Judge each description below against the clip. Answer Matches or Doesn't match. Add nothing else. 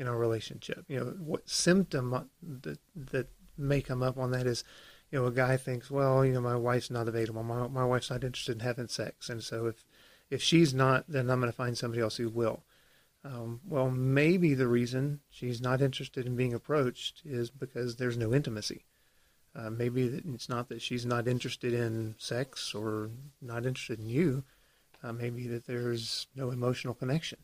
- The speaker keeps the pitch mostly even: Matches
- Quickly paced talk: Doesn't match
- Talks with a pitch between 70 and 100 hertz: Doesn't match